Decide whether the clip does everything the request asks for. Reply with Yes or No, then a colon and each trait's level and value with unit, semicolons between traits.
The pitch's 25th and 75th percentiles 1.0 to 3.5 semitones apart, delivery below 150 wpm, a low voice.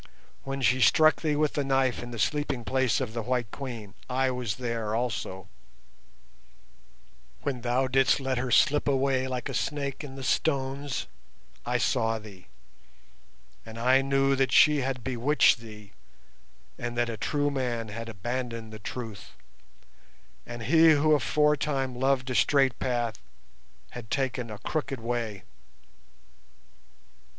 Yes: average, 2.9 semitones; average, 140 wpm; low, 130 Hz